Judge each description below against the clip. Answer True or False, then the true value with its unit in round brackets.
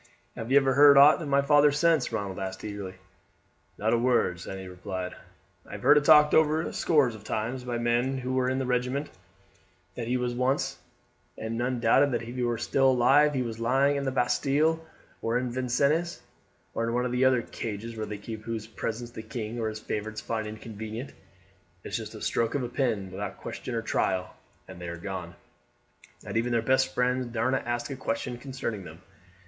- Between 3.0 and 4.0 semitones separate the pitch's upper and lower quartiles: True (3.3 semitones)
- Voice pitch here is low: True (120 Hz)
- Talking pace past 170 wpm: True (200 wpm)